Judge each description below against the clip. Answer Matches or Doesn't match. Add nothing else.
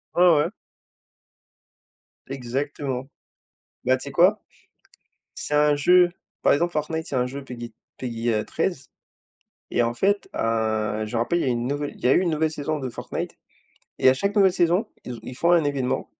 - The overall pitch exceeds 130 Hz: Matches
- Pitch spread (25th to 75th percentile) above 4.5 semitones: Matches